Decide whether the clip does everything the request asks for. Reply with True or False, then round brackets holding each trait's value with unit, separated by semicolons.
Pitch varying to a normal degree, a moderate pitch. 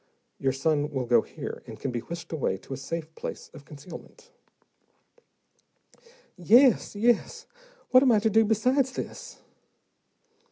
False (8.8 semitones; 170 Hz)